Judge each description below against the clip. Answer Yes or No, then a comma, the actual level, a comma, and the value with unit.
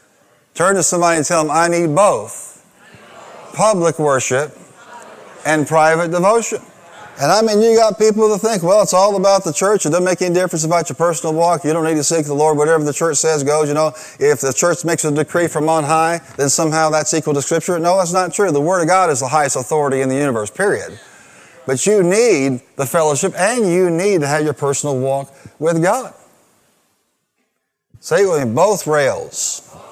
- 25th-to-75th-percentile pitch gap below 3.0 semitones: No, average, 3.4 semitones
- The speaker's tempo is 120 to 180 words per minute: No, fast, 205 wpm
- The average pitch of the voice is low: No, medium, 165 Hz